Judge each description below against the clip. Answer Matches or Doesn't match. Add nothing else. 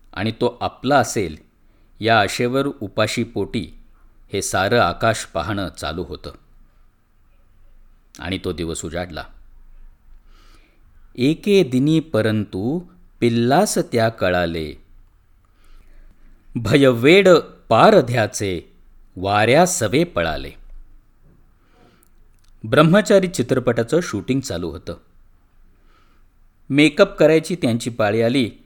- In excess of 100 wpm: Doesn't match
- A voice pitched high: Doesn't match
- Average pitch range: Doesn't match